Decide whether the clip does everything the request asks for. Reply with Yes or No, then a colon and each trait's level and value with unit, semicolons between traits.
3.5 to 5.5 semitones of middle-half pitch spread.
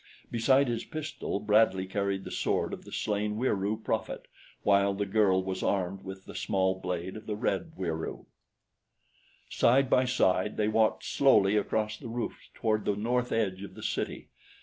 No: average, 2.8 semitones